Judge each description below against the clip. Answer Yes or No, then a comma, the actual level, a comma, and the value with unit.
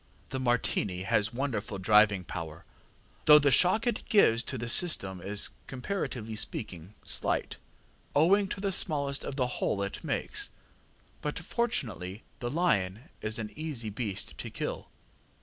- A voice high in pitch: No, low, 120 Hz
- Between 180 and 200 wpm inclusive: No, average, 145 wpm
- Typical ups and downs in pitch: No, wide, 6.7 semitones